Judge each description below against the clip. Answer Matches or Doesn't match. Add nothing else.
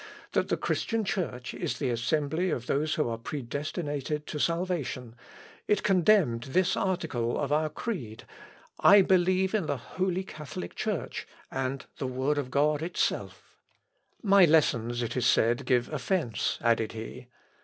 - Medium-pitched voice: Matches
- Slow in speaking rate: Doesn't match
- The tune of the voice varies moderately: Doesn't match